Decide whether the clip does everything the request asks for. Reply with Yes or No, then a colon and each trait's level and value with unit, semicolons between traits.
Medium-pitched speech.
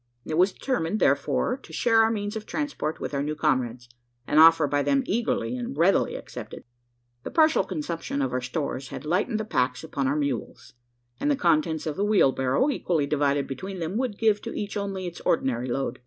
Yes: medium, 165 Hz